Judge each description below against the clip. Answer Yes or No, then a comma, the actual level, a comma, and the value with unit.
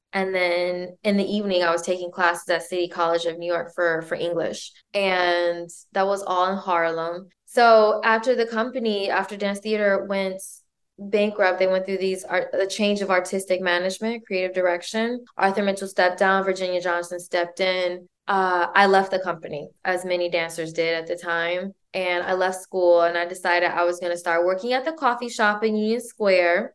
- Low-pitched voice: No, medium, 185 Hz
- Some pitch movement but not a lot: No, narrow, 2.2 semitones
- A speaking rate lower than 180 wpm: No, average, 190 wpm